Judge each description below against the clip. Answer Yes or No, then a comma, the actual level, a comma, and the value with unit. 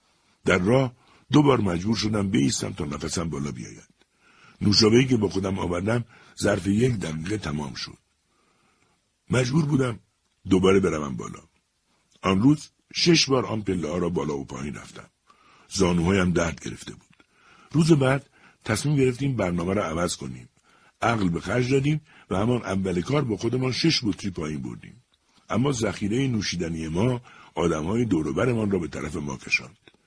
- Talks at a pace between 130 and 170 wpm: Yes, average, 150 wpm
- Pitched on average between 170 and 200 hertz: No, low, 100 Hz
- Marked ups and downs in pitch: Yes, wide, 6.4 semitones